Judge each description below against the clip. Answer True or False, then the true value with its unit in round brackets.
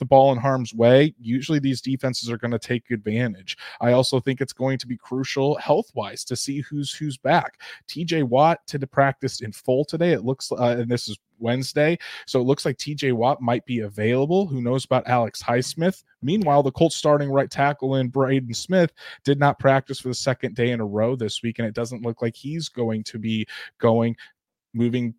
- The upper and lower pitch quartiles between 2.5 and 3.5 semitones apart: True (2.8 semitones)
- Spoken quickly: True (210 wpm)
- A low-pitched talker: True (130 Hz)